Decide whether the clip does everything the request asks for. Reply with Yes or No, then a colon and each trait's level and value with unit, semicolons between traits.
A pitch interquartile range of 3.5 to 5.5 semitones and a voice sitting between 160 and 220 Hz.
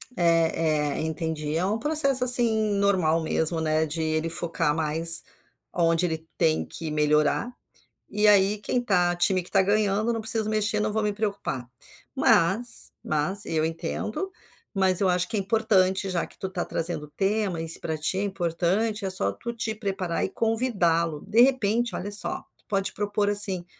Yes: average, 4.4 semitones; high, 190 Hz